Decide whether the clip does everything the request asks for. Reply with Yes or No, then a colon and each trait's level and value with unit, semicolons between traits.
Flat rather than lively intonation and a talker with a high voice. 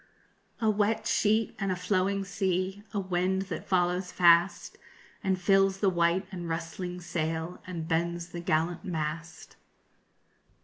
No: narrow, 2.2 semitones; medium, 180 Hz